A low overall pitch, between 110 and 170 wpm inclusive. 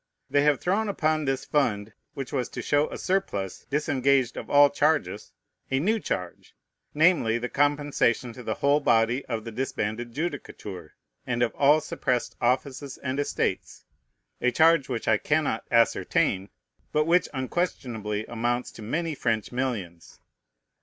Yes: low, 130 Hz; average, 145 wpm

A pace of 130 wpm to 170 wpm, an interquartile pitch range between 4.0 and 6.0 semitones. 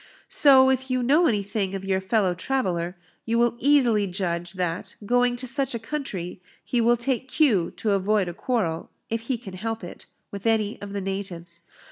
No: average, 185 wpm; average, 4.7 semitones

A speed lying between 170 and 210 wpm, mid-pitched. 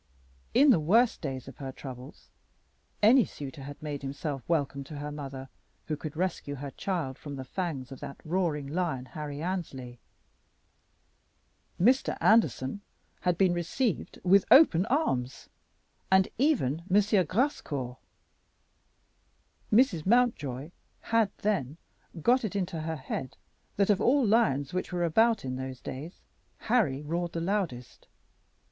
No: slow, 135 wpm; medium, 165 Hz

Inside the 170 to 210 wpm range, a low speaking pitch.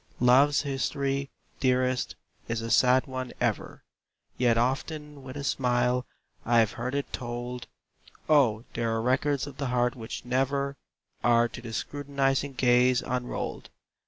No: slow, 135 wpm; low, 125 Hz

